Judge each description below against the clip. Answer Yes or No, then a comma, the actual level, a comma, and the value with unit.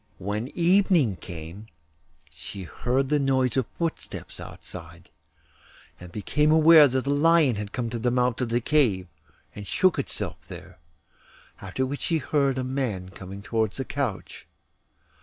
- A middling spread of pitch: No, wide, 6.0 semitones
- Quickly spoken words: No, average, 150 wpm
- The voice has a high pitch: No, low, 125 Hz